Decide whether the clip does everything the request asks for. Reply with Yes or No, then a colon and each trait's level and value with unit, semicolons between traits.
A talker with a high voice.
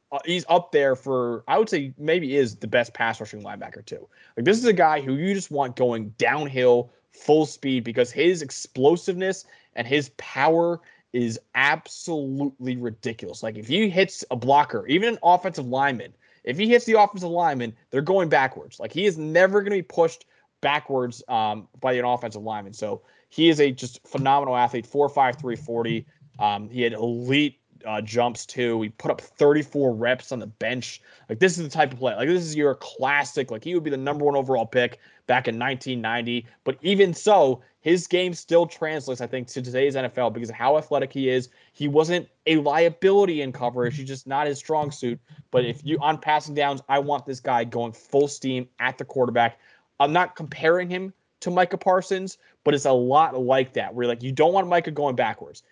No: medium, 140 Hz